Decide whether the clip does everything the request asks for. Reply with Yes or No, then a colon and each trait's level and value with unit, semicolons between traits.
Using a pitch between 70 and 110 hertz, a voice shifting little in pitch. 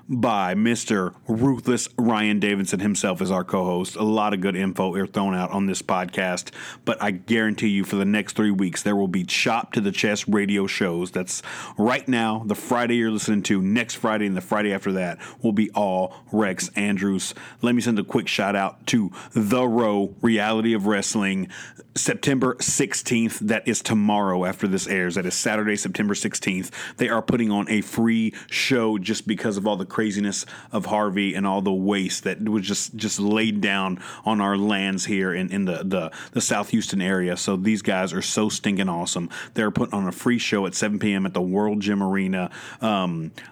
Yes: low, 105 Hz; narrow, 2.1 semitones